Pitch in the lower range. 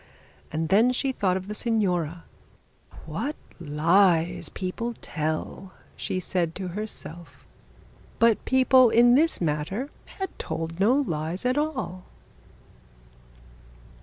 No: high, 190 Hz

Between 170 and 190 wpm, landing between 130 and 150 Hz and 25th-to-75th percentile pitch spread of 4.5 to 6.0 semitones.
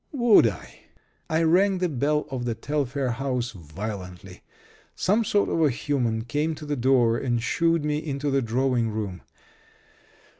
No: average, 155 wpm; low, 135 Hz; average, 4.9 semitones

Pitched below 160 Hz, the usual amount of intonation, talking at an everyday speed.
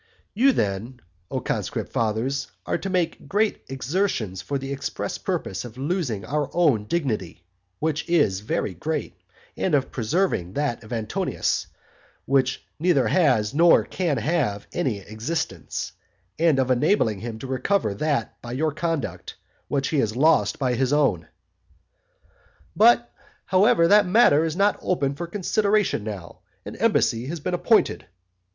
No: medium, 140 Hz; wide, 7.1 semitones; average, 145 wpm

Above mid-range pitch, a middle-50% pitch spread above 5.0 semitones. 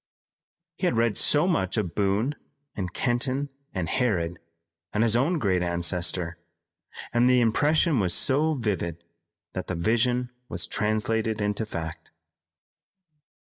No: low, 110 Hz; wide, 5.4 semitones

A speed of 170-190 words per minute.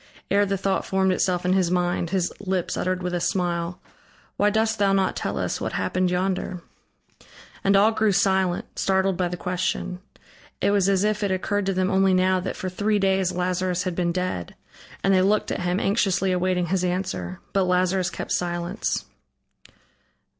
Yes: average, 180 wpm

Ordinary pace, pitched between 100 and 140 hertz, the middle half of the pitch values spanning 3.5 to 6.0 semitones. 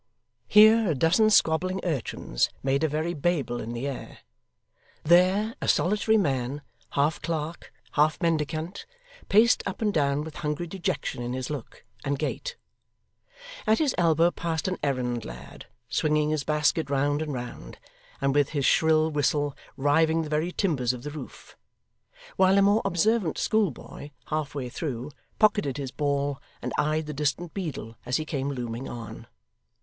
No: average, 155 wpm; medium, 150 Hz; average, 3.8 semitones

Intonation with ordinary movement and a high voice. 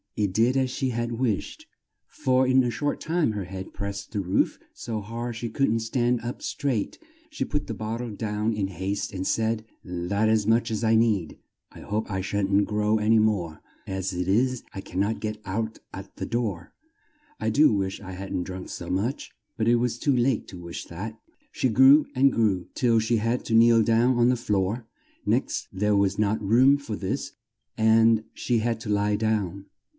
No: average, 3.1 semitones; low, 110 Hz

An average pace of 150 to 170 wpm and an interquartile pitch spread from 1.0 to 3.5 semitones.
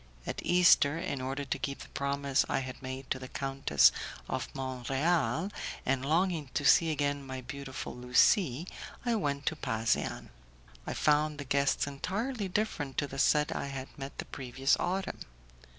Yes: average, 165 wpm; average, 2.8 semitones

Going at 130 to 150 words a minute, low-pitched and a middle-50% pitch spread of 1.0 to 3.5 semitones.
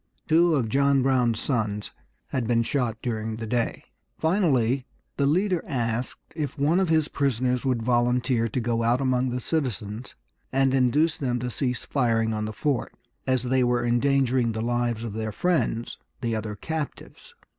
No: average, 165 wpm; low, 125 Hz; average, 3.2 semitones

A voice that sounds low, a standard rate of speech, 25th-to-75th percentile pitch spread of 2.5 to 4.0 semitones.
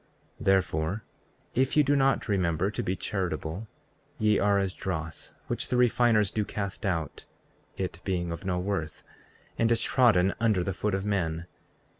Yes: very low, 95 Hz; average, 160 wpm; average, 3.5 semitones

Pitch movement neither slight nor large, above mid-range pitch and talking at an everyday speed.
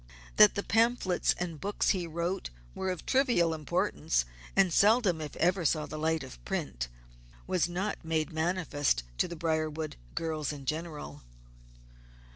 No: average, 3.2 semitones; medium, 165 Hz; average, 145 wpm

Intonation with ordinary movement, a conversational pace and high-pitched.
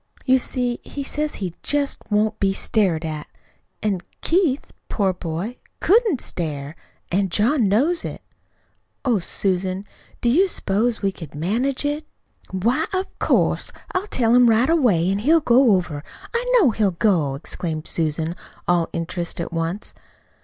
No: wide, 7.5 semitones; average, 150 wpm; high, 210 Hz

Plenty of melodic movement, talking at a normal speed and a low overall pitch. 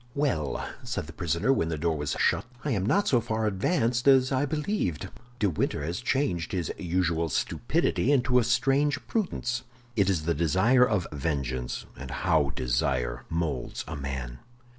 Yes: wide, 8.7 semitones; average, 165 wpm; very low, 90 Hz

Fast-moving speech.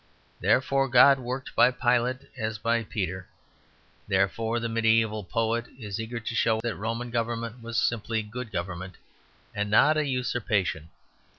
No: average, 140 wpm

